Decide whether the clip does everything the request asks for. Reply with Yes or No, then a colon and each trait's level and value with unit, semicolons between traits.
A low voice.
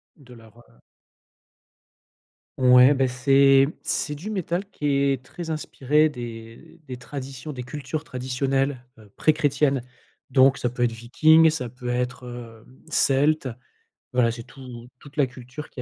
Yes: low, 130 Hz